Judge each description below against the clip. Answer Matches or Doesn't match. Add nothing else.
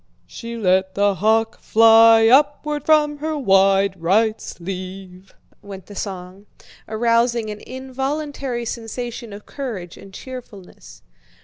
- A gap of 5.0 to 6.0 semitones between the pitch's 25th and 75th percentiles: Doesn't match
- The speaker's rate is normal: Doesn't match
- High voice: Matches